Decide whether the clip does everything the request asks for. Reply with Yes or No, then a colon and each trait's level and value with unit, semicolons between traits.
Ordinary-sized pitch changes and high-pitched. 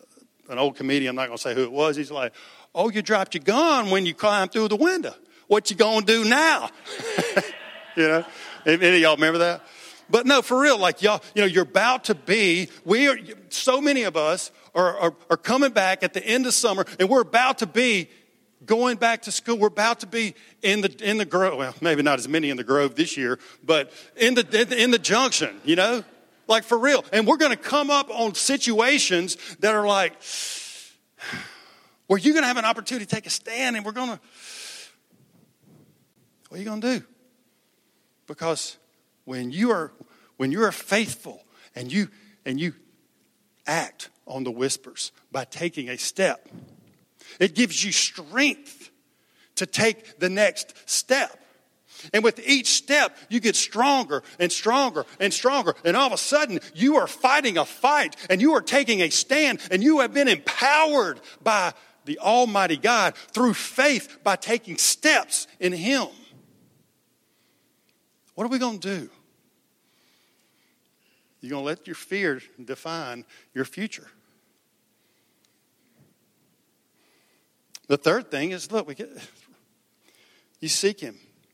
No: wide, 6.6 semitones; high, 215 Hz